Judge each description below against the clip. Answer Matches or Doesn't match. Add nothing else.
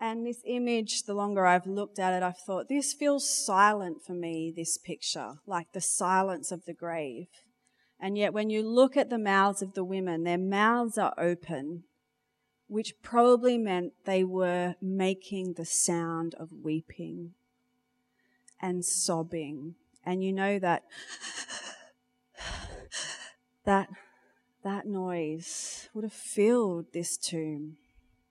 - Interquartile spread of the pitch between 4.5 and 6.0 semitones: Matches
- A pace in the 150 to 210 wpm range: Doesn't match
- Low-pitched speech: Doesn't match